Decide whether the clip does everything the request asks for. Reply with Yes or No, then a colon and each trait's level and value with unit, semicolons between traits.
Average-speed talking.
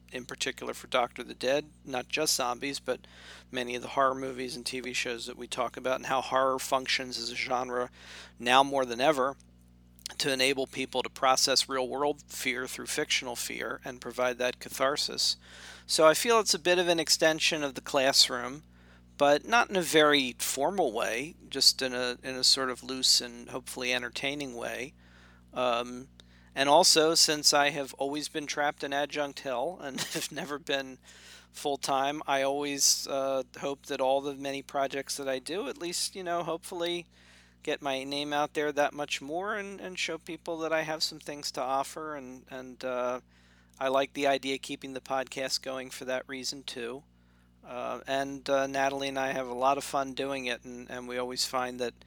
Yes: average, 195 wpm